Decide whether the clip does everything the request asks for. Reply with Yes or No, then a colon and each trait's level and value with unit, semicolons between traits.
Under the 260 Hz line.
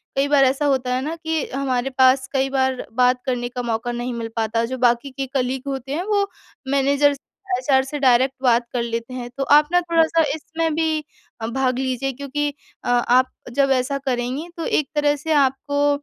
No: very high, 265 Hz